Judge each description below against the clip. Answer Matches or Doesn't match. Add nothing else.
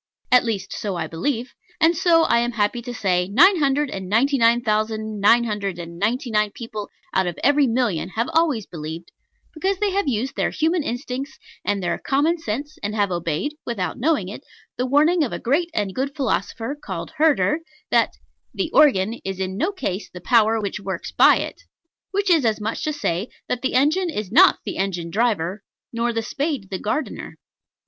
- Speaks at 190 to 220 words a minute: Matches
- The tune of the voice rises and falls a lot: Matches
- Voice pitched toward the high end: Matches